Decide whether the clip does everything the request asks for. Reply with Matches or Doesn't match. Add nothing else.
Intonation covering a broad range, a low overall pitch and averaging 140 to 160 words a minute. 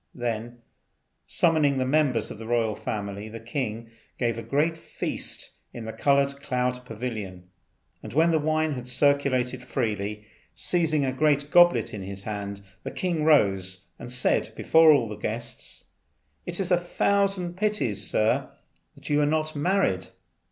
Matches